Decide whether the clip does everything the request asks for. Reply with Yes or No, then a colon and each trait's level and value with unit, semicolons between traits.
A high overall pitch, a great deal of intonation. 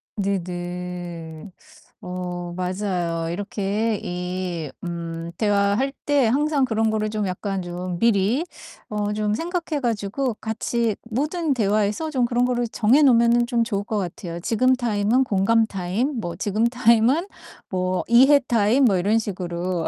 No: high, 210 Hz; average, 4.7 semitones